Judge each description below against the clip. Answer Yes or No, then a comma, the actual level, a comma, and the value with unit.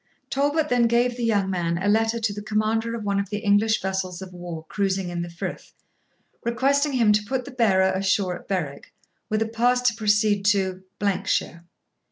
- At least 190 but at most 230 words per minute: Yes, average, 195 wpm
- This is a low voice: No, high, 210 Hz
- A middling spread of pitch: Yes, average, 3.5 semitones